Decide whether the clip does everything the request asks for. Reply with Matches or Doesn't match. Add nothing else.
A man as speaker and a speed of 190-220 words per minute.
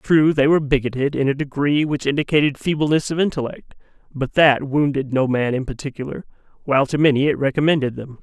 Doesn't match